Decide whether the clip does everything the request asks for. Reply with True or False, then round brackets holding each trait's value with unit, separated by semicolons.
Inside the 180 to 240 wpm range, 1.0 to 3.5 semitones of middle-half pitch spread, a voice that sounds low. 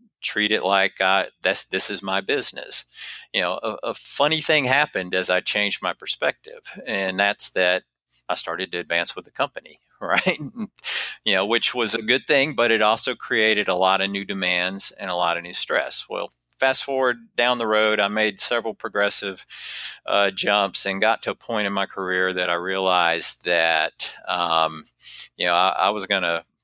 False (195 wpm; 3.9 semitones; 100 Hz)